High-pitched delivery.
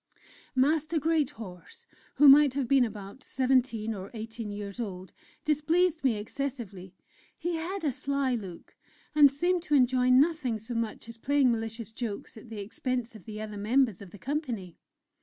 Yes: high, 245 Hz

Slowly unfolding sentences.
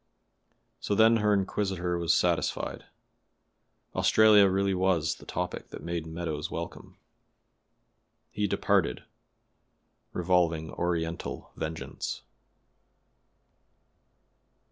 Yes: slow, 80 wpm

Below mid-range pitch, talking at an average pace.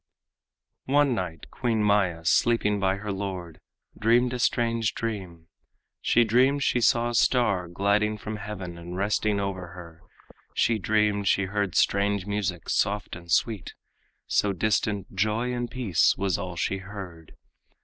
Yes: low, 100 Hz; average, 145 wpm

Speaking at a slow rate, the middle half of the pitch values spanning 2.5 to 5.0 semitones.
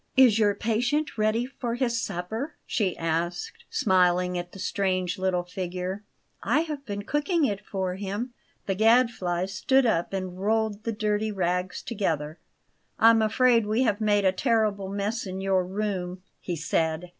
No: average, 155 wpm; average, 3.7 semitones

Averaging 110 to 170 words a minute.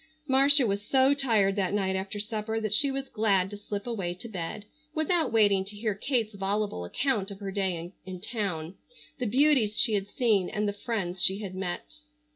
No: average, 195 wpm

